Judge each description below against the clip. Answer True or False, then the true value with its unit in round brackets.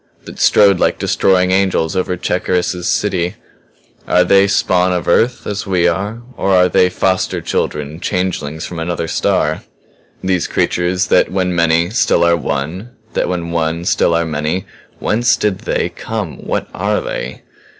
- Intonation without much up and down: True (2.2 semitones)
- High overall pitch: False (90 Hz)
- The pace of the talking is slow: False (155 wpm)